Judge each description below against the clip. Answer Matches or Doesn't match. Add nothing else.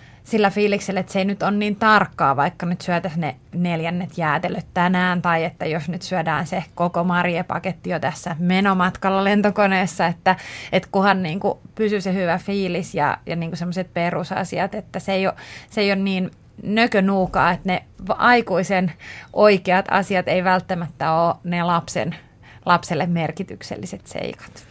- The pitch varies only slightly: Matches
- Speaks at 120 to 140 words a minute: Doesn't match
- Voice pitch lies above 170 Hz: Matches